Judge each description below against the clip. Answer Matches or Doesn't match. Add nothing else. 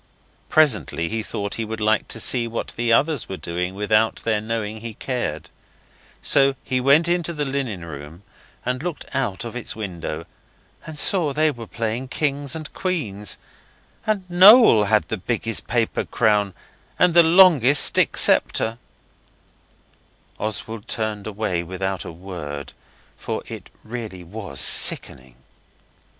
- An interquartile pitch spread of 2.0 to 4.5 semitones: Doesn't match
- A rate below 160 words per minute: Matches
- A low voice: Matches